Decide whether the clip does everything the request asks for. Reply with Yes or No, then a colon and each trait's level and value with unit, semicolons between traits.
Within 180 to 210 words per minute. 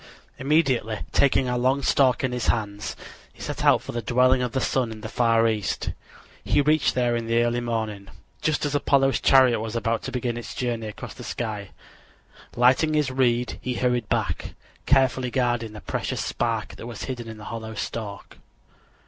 Yes: average, 185 wpm